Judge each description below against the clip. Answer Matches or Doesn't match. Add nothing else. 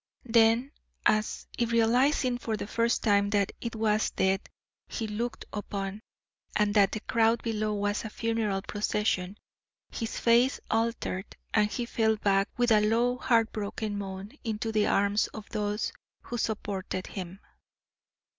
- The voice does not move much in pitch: Matches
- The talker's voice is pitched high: Matches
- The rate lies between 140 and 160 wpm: Matches